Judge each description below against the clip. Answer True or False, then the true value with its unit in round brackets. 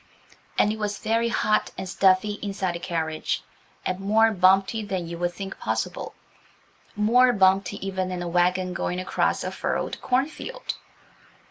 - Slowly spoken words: False (150 wpm)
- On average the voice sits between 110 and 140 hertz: False (195 Hz)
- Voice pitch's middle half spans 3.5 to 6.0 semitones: False (2.9 semitones)